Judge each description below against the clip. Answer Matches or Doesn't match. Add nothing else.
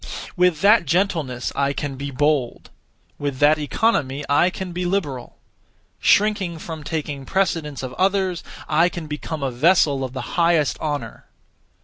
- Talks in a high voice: Doesn't match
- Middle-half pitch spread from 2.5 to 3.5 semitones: Doesn't match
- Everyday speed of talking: Matches